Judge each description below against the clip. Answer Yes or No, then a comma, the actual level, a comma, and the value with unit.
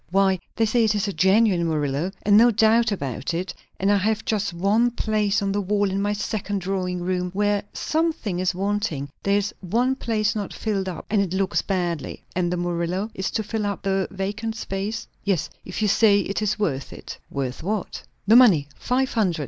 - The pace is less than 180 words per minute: No, fast, 205 wpm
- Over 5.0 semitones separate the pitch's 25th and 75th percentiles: No, average, 2.9 semitones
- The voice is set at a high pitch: Yes, high, 200 Hz